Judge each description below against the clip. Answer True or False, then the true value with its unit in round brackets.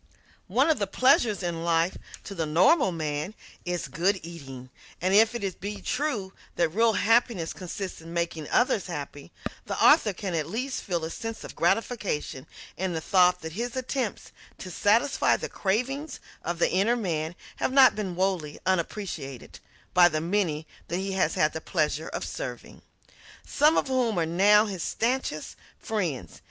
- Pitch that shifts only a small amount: False (5.2 semitones)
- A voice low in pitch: False (185 Hz)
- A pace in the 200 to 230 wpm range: False (165 wpm)